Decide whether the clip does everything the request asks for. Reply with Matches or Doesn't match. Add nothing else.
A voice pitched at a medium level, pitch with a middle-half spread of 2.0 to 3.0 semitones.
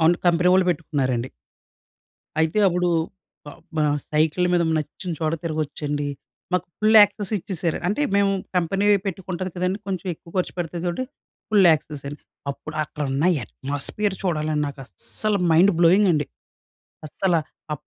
Doesn't match